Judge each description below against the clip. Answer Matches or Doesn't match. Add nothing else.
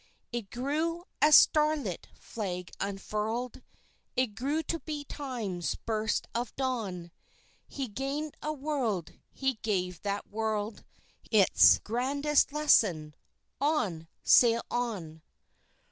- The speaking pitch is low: Doesn't match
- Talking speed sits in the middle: Doesn't match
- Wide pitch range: Matches